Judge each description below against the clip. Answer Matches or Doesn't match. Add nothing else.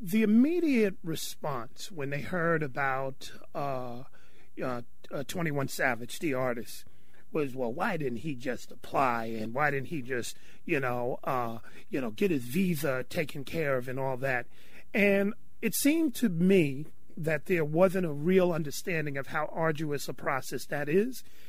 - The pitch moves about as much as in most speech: Doesn't match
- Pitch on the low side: Doesn't match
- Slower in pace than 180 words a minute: Matches